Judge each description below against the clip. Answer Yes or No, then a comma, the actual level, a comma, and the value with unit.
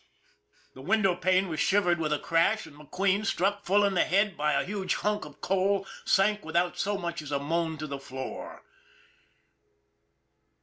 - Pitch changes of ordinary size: Yes, average, 4.3 semitones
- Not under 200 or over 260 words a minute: No, average, 180 wpm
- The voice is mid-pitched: Yes, medium, 180 Hz